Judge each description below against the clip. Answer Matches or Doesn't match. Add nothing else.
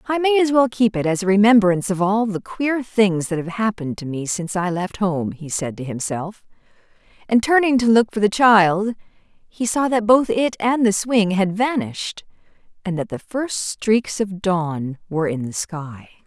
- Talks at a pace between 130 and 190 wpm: Doesn't match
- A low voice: Doesn't match